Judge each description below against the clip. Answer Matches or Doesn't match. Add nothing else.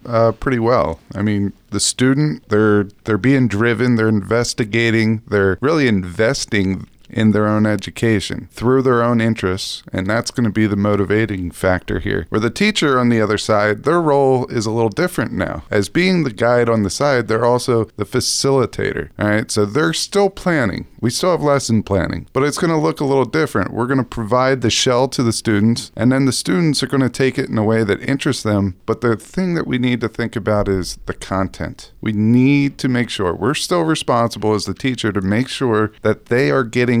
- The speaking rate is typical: Doesn't match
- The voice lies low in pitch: Matches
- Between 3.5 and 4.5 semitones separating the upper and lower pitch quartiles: Matches